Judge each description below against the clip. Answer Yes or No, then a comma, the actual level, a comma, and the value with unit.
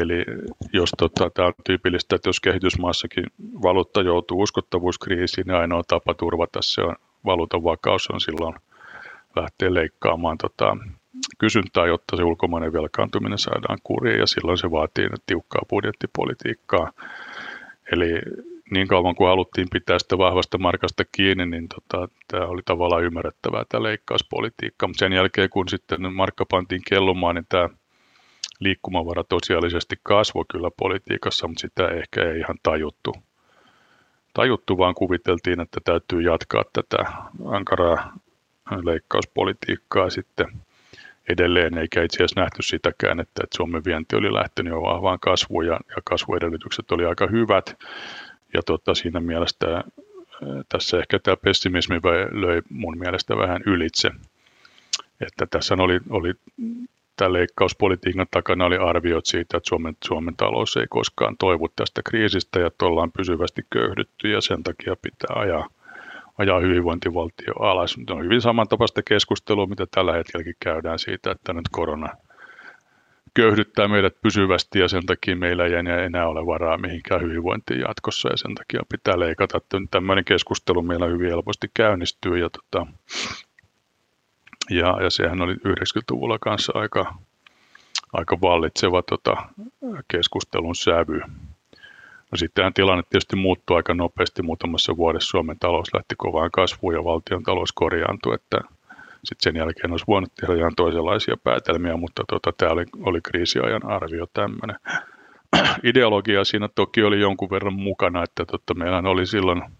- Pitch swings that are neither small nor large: No, narrow, 2.3 semitones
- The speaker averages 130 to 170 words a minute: Yes, average, 135 wpm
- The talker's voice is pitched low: Yes, very low, 90 Hz